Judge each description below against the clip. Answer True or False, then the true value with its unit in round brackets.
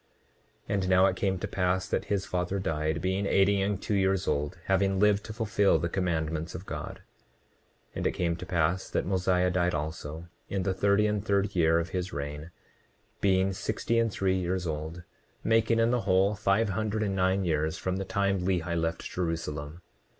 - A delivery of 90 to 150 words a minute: False (195 wpm)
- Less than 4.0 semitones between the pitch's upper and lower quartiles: True (2.7 semitones)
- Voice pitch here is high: False (95 Hz)